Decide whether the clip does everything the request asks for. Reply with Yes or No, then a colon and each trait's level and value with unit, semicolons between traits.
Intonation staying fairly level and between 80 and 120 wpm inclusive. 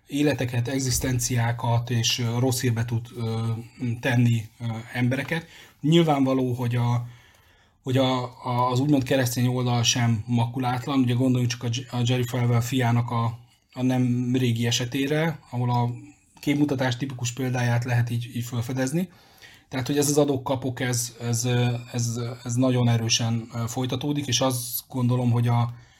No: narrow, 1.7 semitones; average, 135 wpm